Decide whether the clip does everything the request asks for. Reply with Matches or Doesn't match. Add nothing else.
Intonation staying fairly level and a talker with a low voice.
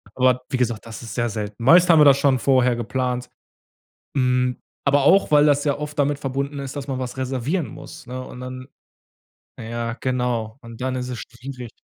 Matches